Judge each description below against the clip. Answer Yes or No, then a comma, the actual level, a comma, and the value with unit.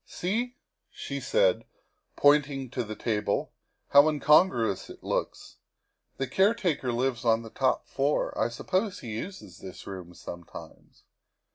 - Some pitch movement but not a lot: No, wide, 8.2 semitones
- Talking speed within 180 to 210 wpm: No, average, 145 wpm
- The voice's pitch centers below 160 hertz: Yes, low, 135 Hz